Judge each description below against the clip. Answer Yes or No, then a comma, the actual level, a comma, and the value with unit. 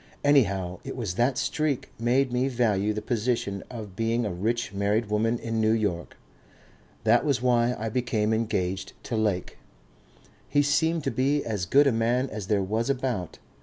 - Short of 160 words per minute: No, average, 170 wpm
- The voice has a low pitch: Yes, low, 115 Hz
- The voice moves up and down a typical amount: Yes, average, 3.3 semitones